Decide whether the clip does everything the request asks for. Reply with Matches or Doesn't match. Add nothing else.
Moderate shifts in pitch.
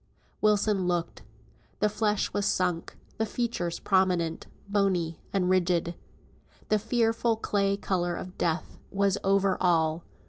Matches